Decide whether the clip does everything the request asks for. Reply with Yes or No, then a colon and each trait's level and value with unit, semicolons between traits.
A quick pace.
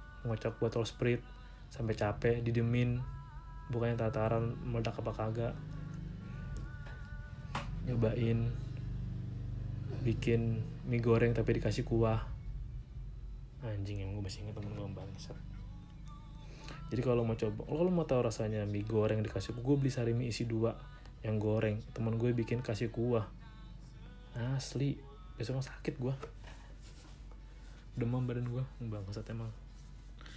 No: average, 120 wpm